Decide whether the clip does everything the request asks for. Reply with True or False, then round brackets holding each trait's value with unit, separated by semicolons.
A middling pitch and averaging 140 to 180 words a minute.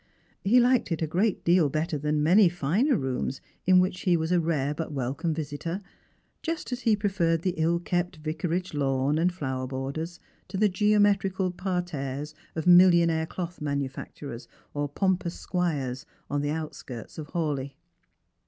True (165 Hz; 155 wpm)